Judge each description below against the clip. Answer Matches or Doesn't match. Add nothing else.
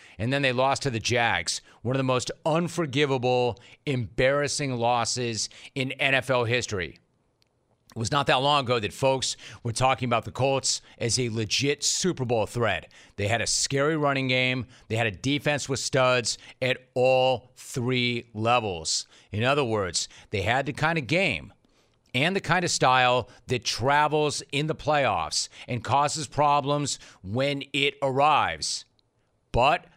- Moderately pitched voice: Doesn't match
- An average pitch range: Matches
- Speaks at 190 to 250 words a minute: Doesn't match